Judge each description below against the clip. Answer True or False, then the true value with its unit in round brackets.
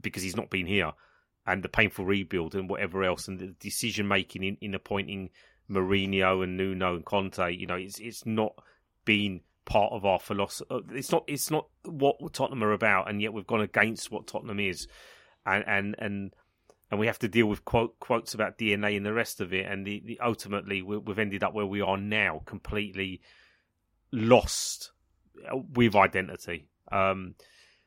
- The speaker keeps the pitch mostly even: True (2.3 semitones)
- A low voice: True (100 Hz)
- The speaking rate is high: False (180 wpm)